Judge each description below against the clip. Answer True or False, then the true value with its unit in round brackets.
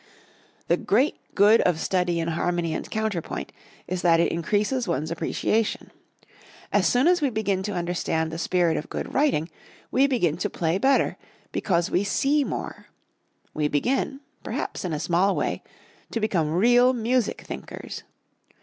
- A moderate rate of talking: True (155 wpm)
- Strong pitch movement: True (6.2 semitones)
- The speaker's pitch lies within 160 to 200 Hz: True (190 Hz)